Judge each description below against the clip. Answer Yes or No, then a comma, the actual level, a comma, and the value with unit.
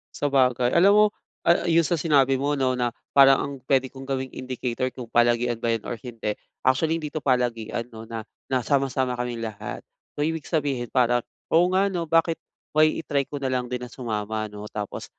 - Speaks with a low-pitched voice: Yes, low, 130 Hz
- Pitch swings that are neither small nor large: Yes, average, 3.4 semitones